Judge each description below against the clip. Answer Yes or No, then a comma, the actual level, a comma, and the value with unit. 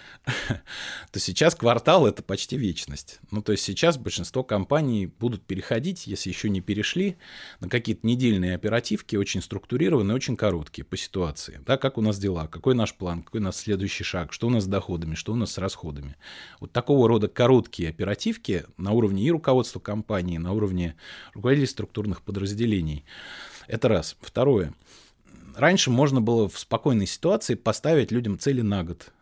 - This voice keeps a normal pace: No, fast, 165 wpm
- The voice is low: Yes, low, 105 Hz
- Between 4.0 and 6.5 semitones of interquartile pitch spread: Yes, average, 4.7 semitones